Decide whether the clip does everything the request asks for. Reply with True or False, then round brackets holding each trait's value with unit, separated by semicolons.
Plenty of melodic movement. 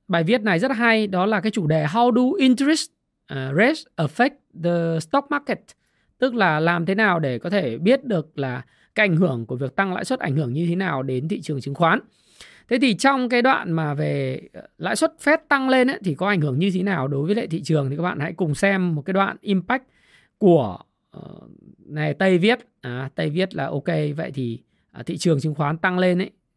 True (7.0 semitones)